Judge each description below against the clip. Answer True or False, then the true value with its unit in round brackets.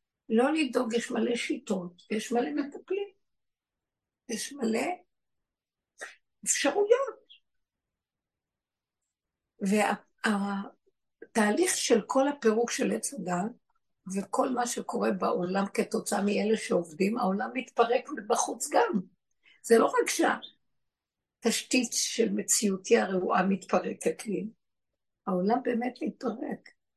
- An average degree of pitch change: True (4.2 semitones)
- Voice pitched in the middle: False (235 Hz)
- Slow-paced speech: True (95 wpm)